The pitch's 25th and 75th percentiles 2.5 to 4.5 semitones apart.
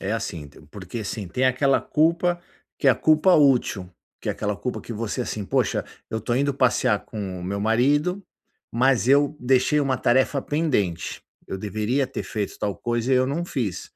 No: average, 5.3 semitones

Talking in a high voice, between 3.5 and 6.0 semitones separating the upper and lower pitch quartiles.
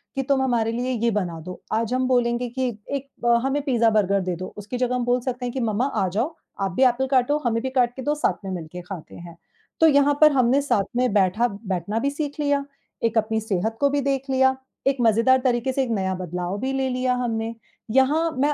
Yes: high, 245 Hz; average, 4.1 semitones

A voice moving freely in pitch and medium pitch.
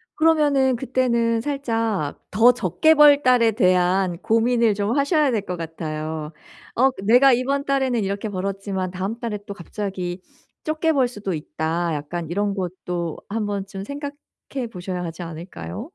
No: wide, 6.0 semitones; high, 205 Hz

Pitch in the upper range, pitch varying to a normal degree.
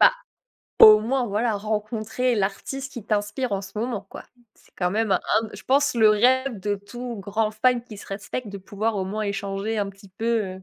Yes: high, 215 Hz; average, 3.0 semitones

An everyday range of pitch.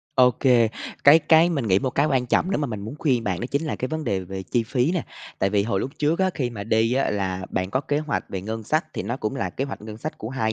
No: wide, 5.7 semitones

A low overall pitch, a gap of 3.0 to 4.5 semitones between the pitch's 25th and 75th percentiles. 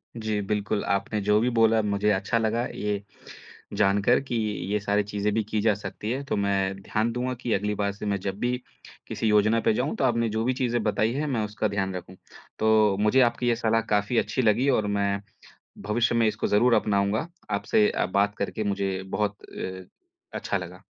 No: low, 105 Hz; narrow, 2.4 semitones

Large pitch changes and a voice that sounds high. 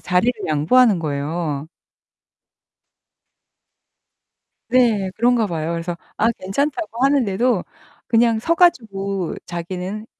Yes: wide, 5.9 semitones; high, 200 Hz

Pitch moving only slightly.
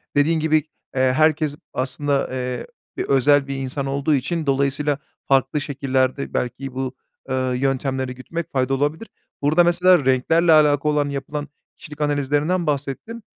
Yes: narrow, 2.3 semitones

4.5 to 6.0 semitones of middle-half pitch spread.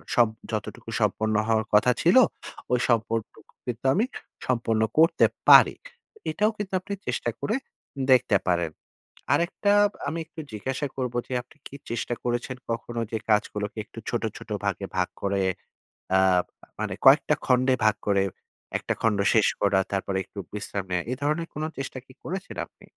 Yes: average, 4.8 semitones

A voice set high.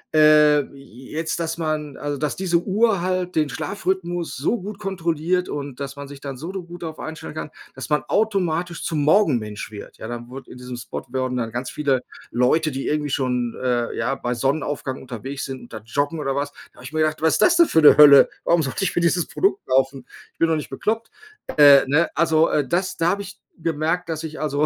No: medium, 150 Hz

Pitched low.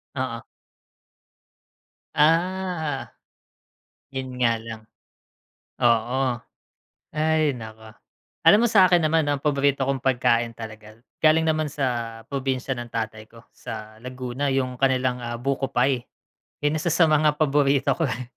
Yes: low, 130 Hz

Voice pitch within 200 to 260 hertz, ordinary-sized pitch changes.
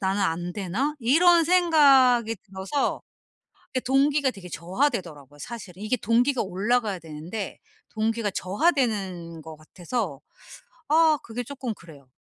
No: high, 220 Hz; wide, 6.8 semitones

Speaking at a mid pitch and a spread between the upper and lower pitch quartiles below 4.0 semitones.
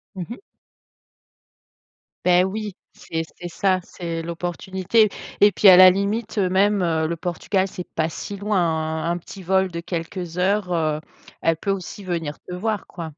Yes: medium, 180 Hz; average, 2.8 semitones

